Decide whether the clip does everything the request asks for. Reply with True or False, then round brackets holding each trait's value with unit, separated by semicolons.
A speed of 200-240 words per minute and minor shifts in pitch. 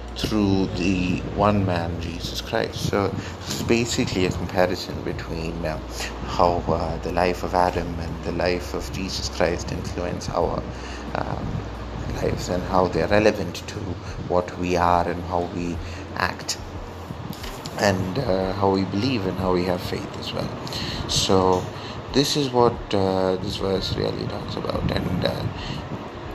False (150 wpm; 2.2 semitones)